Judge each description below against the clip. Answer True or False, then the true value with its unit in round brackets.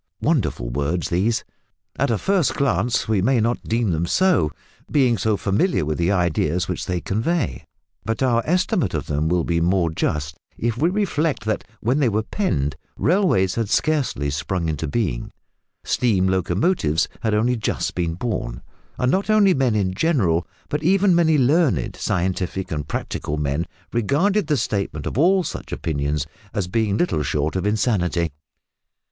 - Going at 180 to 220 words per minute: False (165 wpm)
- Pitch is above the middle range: False (105 Hz)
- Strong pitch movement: True (8.5 semitones)